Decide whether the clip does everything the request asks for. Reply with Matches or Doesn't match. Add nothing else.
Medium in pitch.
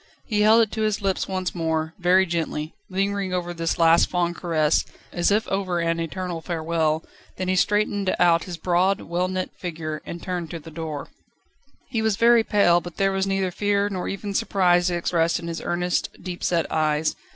Matches